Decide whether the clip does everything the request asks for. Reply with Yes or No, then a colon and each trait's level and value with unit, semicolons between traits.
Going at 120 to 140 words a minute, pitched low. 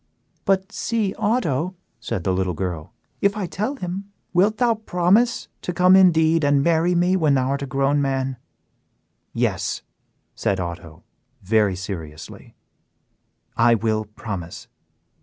No: slow, 135 wpm; medium, 145 Hz